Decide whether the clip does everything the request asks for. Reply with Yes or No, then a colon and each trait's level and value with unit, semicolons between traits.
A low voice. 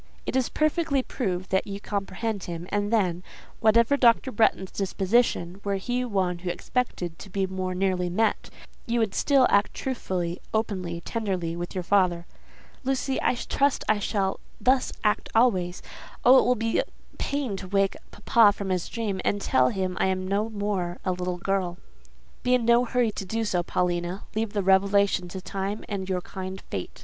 No: high, 195 Hz